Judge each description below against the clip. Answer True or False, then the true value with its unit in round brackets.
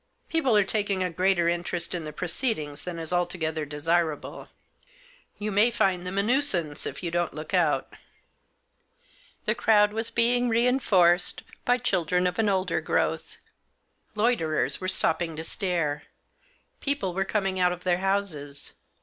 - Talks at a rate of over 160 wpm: False (150 wpm)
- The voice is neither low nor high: True (180 Hz)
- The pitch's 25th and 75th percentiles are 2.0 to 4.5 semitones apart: True (3.8 semitones)